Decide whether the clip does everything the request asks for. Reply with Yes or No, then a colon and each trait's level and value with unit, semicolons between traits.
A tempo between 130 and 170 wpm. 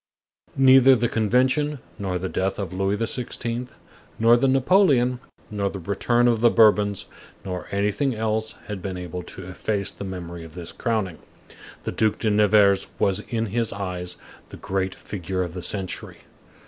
Yes: average, 160 wpm